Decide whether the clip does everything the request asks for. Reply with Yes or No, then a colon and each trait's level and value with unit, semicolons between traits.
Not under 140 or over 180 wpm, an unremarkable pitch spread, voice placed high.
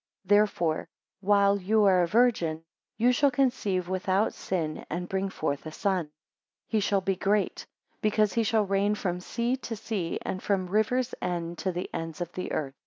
No: average, 190 wpm; average, 3.3 semitones; high, 195 Hz